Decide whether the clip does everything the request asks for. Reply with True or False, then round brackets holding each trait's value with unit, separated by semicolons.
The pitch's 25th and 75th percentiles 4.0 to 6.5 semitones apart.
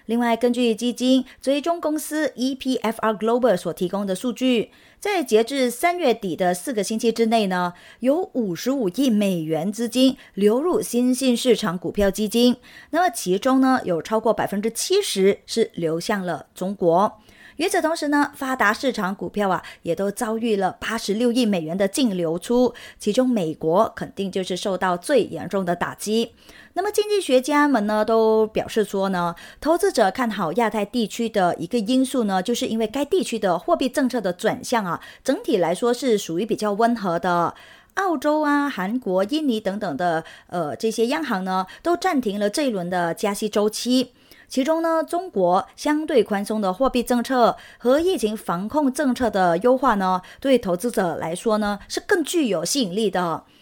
True (5.3 semitones)